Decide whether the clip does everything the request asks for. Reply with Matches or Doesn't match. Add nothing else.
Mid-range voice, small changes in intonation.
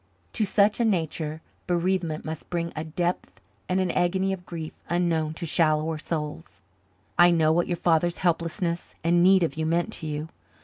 Matches